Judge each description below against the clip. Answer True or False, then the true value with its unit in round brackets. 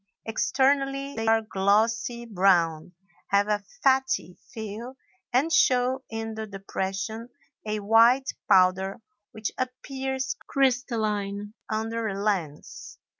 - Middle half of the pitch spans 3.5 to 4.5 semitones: True (4.2 semitones)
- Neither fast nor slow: False (105 wpm)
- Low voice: False (225 Hz)